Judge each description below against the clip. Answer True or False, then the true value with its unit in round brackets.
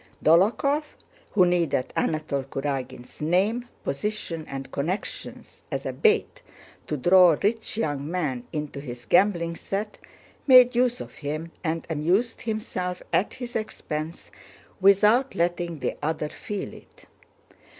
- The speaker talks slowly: True (125 wpm)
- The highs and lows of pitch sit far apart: True (5.8 semitones)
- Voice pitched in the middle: True (175 Hz)